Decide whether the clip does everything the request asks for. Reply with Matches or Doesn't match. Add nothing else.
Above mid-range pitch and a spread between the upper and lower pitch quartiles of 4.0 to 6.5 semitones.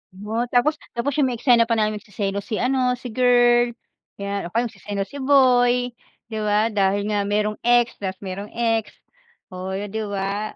Doesn't match